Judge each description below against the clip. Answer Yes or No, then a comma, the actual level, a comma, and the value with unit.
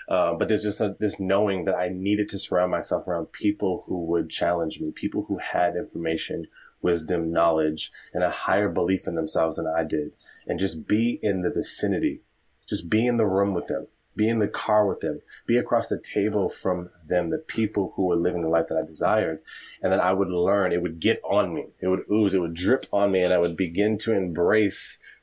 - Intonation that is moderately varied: Yes, average, 3.3 semitones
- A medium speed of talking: No, fast, 220 wpm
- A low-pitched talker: Yes, very low, 95 Hz